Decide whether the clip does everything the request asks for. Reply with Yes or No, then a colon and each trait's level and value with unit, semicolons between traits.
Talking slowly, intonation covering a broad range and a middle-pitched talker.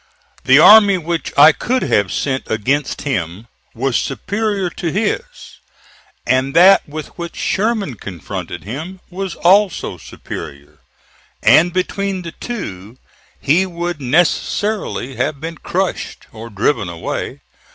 Yes: slow, 120 wpm; wide, 7.4 semitones; medium, 160 Hz